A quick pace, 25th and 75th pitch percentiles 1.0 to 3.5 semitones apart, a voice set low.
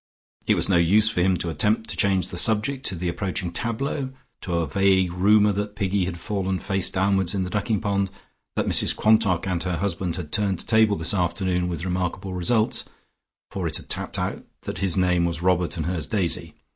Yes: fast, 210 wpm; average, 2.7 semitones; very low, 95 Hz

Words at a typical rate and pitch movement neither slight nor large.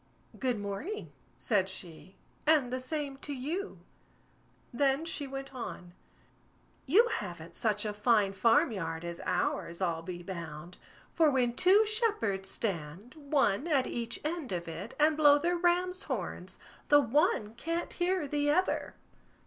No: average, 145 wpm; wide, 8.3 semitones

